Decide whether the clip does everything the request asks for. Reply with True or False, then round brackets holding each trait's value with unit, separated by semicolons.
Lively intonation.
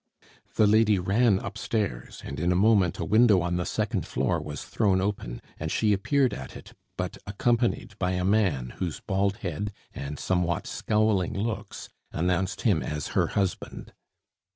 False (3.6 semitones)